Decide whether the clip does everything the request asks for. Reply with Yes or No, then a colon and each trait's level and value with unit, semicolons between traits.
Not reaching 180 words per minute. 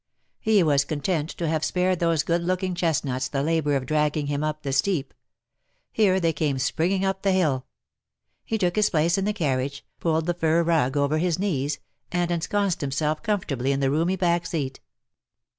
No: average, 190 wpm